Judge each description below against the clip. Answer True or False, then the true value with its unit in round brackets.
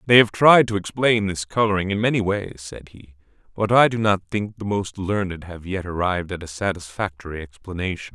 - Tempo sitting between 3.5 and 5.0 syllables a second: False (5.5 syllables/s)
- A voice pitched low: True (95 Hz)